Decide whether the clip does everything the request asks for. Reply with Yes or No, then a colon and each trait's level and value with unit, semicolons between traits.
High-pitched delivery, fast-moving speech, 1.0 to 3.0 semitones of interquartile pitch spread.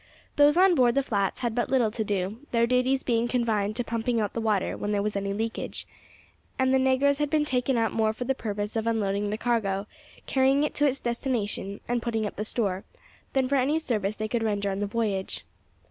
No: high, 230 Hz; fast, 225 wpm; average, 3.9 semitones